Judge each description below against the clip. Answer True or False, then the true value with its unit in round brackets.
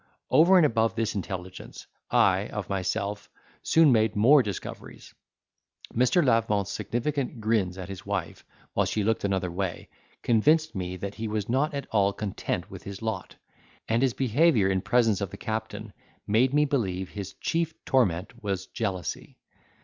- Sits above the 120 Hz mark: False (110 Hz)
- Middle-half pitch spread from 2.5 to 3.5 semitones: False (4.5 semitones)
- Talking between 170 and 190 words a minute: False (155 wpm)